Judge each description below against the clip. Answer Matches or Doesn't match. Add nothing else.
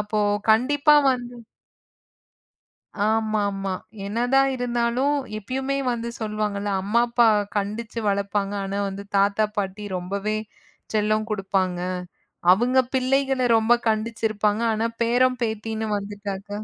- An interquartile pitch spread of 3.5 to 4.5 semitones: Doesn't match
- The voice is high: Matches